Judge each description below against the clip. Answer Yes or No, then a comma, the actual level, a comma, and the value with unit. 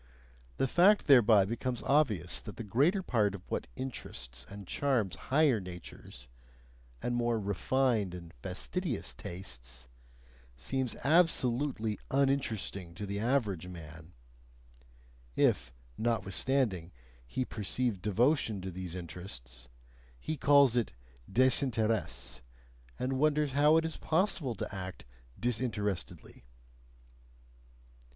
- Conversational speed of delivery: No, slow, 105 wpm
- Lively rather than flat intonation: Yes, wide, 6.5 semitones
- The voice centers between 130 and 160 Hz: No, low, 110 Hz